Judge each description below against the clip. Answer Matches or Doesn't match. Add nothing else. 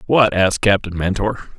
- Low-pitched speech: Matches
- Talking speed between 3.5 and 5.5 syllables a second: Matches